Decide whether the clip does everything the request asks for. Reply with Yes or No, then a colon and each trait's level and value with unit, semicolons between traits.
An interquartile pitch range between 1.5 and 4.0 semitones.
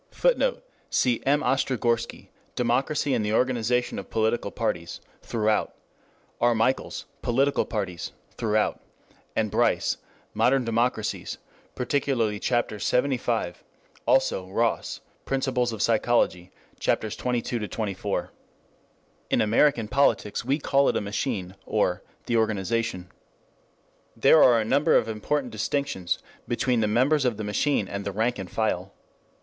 Yes: average, 3.3 semitones